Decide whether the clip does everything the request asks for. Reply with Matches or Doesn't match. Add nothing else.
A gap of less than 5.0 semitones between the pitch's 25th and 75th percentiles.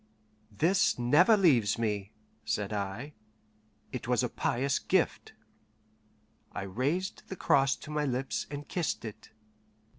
Doesn't match